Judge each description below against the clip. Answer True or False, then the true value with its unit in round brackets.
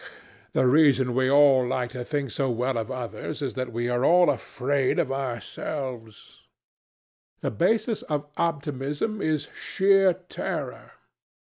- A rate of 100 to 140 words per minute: True (135 wpm)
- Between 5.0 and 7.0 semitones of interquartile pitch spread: False (3.4 semitones)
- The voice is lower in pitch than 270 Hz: True (135 Hz)